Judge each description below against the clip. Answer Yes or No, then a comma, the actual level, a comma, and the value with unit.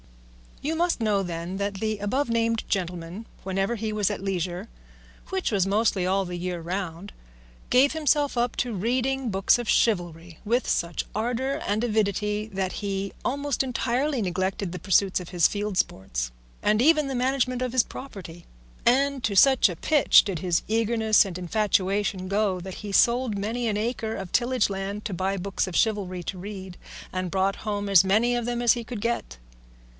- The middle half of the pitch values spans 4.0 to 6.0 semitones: Yes, average, 4.3 semitones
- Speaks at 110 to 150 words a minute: No, average, 180 wpm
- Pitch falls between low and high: No, high, 205 Hz